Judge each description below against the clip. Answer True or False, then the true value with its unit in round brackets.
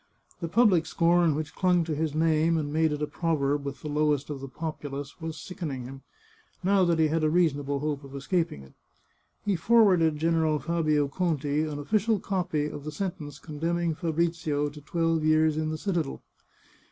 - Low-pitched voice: False (155 Hz)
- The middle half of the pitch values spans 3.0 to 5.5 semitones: False (2.4 semitones)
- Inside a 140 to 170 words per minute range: False (180 wpm)